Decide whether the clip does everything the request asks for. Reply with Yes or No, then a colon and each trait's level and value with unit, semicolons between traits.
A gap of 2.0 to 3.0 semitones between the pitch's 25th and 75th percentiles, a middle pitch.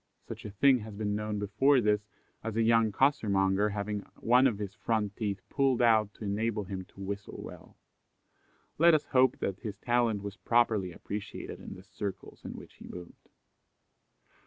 No: narrow, 2.6 semitones; low, 105 Hz